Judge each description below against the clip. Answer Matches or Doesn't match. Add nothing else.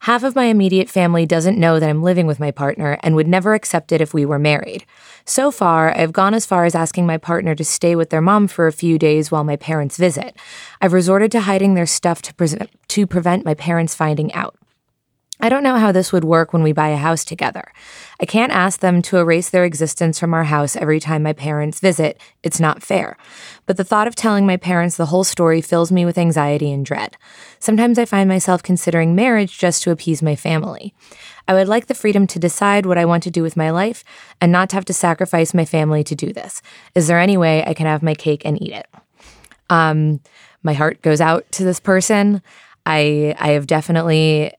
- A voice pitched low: Doesn't match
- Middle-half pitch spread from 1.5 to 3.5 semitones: Matches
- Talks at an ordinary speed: Doesn't match